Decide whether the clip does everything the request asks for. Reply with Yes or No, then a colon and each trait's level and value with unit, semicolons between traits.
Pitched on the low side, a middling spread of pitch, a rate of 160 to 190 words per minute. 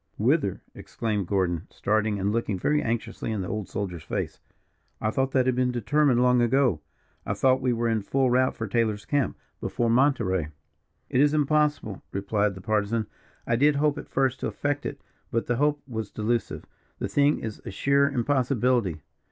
Yes: low, 120 Hz; average, 4.3 semitones; average, 180 wpm